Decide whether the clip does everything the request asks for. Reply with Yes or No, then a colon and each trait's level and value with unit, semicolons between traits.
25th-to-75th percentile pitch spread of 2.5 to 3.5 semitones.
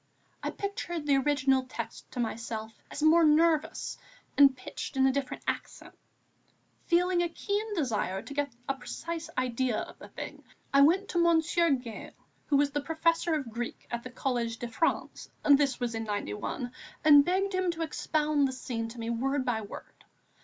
No: average, 5.0 semitones